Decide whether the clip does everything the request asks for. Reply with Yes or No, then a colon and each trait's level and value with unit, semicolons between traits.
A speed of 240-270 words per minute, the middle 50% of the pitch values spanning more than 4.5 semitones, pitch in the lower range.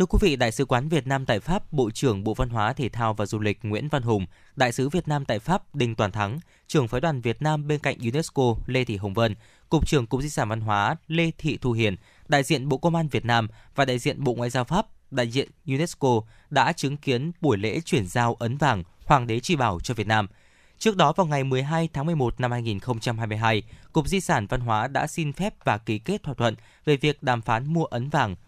Yes: average, 245 wpm; average, 5.1 semitones; low, 125 Hz